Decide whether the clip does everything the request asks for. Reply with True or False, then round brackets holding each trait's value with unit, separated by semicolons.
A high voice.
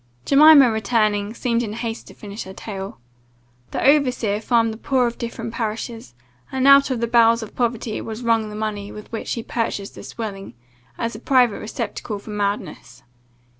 True (225 Hz)